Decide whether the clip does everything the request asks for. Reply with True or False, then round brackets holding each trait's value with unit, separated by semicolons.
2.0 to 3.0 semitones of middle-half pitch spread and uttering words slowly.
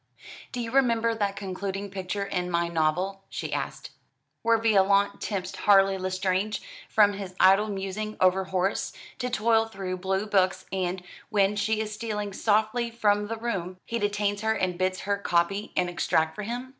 False (2.5 semitones; 170 wpm)